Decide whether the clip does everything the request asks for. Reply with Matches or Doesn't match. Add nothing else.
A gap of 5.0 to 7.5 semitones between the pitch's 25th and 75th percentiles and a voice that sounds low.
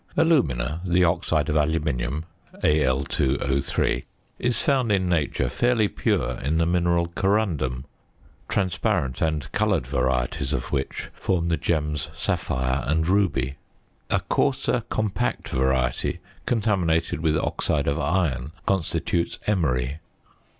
Matches